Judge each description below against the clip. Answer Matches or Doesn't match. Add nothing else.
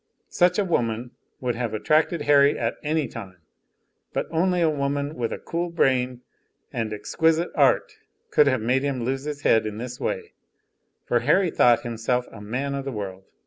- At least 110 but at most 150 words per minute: Doesn't match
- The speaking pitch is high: Doesn't match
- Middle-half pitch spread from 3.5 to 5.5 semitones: Matches